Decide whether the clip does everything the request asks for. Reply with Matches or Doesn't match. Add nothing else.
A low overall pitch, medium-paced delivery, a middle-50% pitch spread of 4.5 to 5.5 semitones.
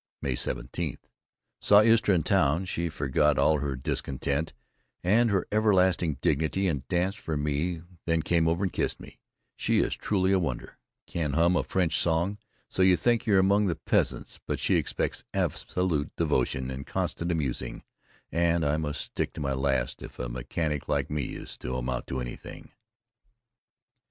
Matches